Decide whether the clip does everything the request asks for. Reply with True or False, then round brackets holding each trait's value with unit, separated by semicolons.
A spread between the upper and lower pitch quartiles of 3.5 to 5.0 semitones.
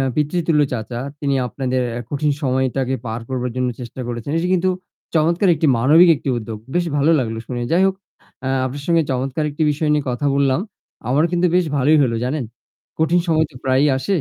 True (4.0 semitones)